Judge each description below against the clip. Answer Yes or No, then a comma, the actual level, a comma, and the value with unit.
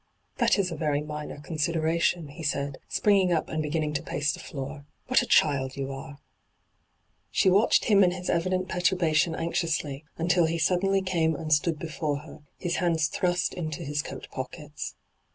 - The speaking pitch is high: No, medium, 160 Hz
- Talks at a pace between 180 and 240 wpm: Yes, average, 190 wpm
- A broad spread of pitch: No, average, 3.1 semitones